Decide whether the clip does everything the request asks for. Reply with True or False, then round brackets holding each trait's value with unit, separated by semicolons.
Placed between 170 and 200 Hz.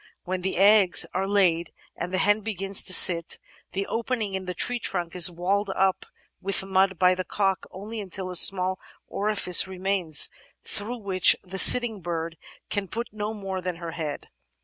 True (190 Hz)